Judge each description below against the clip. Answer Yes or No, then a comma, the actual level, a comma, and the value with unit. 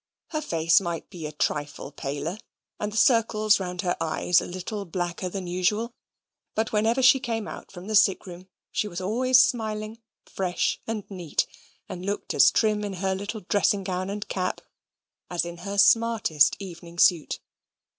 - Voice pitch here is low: No, high, 195 Hz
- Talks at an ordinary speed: Yes, average, 170 wpm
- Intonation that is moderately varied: Yes, average, 3.5 semitones